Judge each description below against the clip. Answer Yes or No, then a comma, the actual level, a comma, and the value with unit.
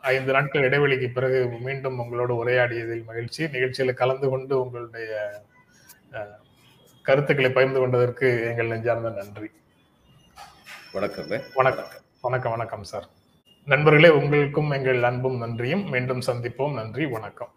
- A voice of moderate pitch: No, low, 125 Hz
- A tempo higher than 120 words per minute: No, average, 110 wpm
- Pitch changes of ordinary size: No, narrow, 2.2 semitones